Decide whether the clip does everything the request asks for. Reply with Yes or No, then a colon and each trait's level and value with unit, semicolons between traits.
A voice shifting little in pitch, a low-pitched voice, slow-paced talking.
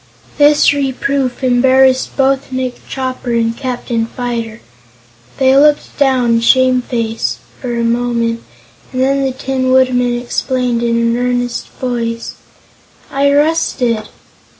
No: narrow, 2.0 semitones; very high, 250 Hz; slow, 115 wpm